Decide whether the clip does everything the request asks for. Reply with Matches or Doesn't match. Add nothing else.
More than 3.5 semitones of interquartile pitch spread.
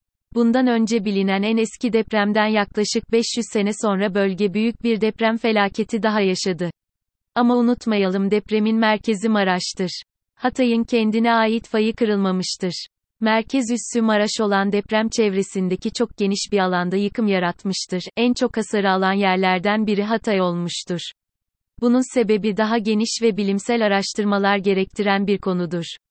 Doesn't match